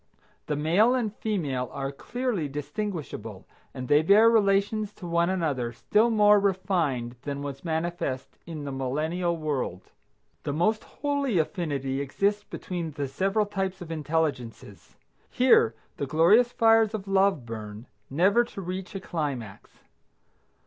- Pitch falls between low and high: Yes, medium, 170 Hz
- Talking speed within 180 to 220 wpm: No, slow, 135 wpm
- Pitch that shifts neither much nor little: No, wide, 6.4 semitones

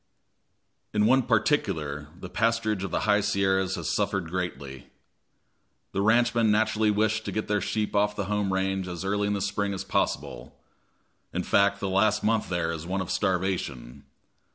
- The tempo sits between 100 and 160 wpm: No, average, 170 wpm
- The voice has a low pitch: Yes, low, 100 Hz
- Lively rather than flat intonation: No, narrow, 2.4 semitones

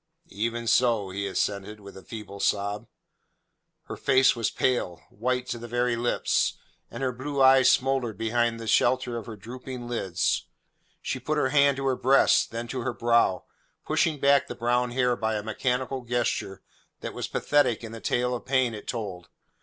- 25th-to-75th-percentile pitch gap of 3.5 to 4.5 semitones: No, average, 2.8 semitones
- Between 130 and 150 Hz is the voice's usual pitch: No, low, 120 Hz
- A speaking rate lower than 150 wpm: No, average, 180 wpm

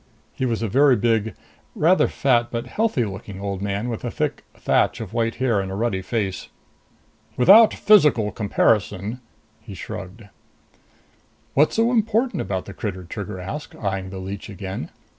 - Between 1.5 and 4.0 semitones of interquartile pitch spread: No, average, 4.4 semitones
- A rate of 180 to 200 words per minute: No, average, 165 wpm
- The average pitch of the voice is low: Yes, low, 110 Hz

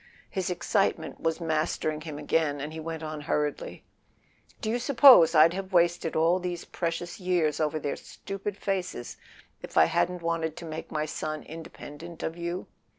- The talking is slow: No, average, 170 wpm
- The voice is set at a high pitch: No, medium, 165 Hz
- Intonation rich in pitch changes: No, narrow, 2.5 semitones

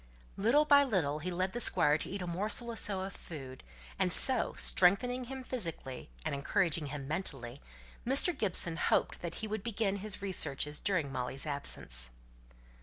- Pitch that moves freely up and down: Yes, wide, 7.0 semitones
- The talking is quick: No, average, 170 wpm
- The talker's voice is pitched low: No, medium, 185 Hz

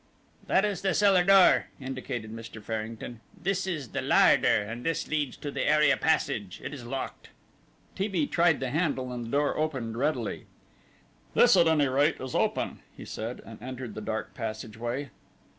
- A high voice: No, low, 135 Hz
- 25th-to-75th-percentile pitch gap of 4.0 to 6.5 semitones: Yes, wide, 5.6 semitones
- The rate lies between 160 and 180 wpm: Yes, average, 170 wpm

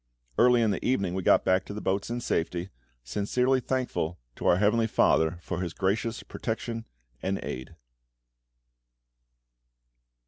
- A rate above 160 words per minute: No, average, 140 wpm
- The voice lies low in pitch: Yes, low, 100 Hz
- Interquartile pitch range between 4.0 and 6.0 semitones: Yes, average, 4.4 semitones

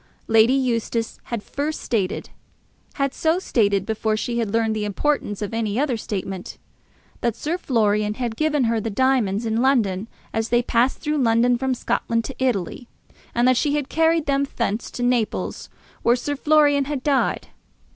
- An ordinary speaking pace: Yes, average, 170 wpm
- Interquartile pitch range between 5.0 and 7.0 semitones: No, average, 3.8 semitones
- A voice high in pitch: Yes, high, 240 Hz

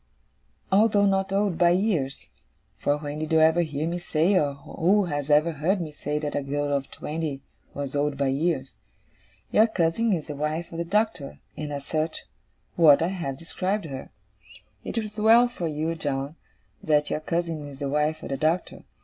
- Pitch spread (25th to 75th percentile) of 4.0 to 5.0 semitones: No, average, 3.6 semitones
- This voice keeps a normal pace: Yes, average, 190 wpm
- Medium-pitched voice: Yes, medium, 155 Hz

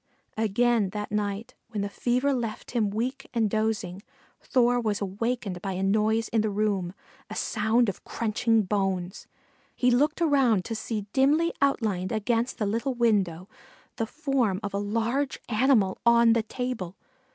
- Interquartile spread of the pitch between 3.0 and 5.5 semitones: Yes, average, 3.3 semitones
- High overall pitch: Yes, high, 220 Hz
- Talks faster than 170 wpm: No, average, 155 wpm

